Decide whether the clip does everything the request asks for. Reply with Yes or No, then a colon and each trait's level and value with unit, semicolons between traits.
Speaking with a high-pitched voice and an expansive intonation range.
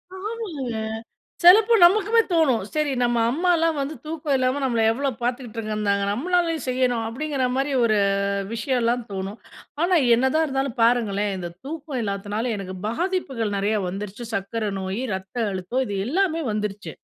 Yes: high, 245 Hz; wide, 6.7 semitones